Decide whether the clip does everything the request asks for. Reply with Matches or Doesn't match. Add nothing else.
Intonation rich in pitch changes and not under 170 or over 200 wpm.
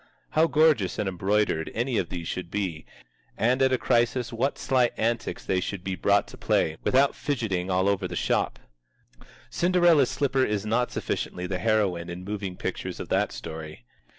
Matches